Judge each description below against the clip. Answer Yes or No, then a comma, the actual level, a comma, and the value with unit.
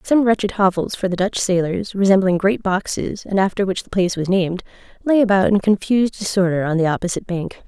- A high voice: Yes, high, 195 Hz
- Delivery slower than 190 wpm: No, fast, 205 wpm